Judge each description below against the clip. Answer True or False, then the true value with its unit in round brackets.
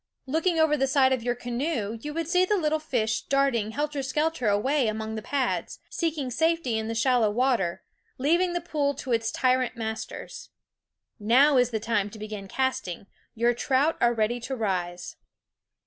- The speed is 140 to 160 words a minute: False (170 wpm)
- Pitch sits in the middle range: False (255 Hz)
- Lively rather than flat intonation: False (5.0 semitones)